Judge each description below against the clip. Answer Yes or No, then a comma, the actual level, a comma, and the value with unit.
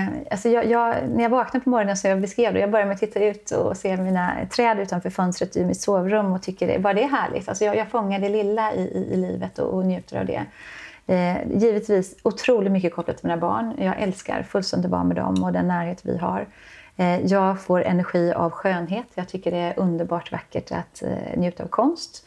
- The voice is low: No, high, 195 Hz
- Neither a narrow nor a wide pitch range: Yes, average, 3.7 semitones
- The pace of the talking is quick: Yes, fast, 225 wpm